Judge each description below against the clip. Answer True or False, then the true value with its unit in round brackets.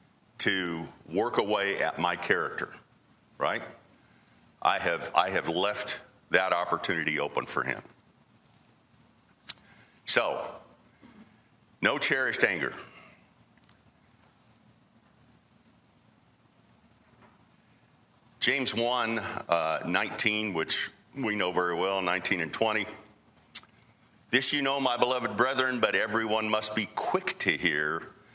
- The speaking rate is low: True (95 wpm)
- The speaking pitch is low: True (110 Hz)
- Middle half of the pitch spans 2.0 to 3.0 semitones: True (2.6 semitones)